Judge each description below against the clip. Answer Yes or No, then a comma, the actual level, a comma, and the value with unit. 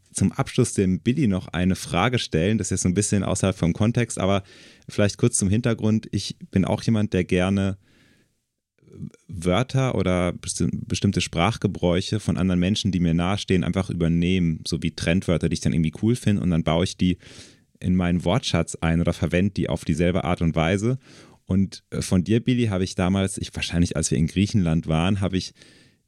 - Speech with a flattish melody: No, average, 3.2 semitones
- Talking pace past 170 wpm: Yes, fast, 190 wpm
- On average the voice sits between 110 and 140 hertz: No, very low, 95 Hz